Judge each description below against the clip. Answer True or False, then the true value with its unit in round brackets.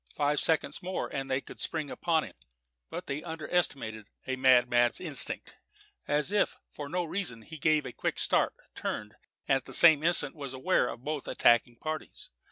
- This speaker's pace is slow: False (180 wpm)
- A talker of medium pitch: True (145 Hz)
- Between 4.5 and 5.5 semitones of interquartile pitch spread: False (3.8 semitones)